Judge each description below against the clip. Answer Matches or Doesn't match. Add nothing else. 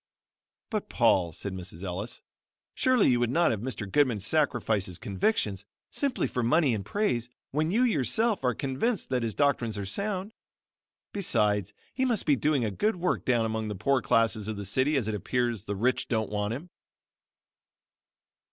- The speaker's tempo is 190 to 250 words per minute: Doesn't match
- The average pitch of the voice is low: Matches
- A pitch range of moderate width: Doesn't match